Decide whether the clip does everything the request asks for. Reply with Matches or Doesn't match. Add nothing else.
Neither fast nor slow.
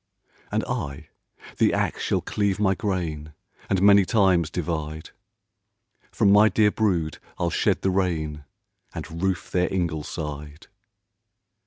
Doesn't match